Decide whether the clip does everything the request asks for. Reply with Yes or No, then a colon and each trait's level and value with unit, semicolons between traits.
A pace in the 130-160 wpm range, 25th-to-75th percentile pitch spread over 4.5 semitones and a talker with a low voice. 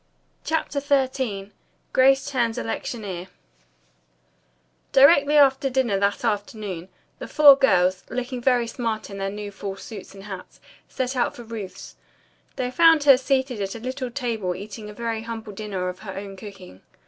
No: average, 155 wpm; average, 4.9 semitones; high, 225 Hz